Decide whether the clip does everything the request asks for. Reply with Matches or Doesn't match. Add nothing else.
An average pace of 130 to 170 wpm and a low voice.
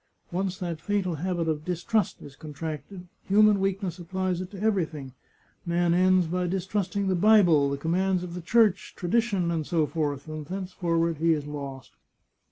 Doesn't match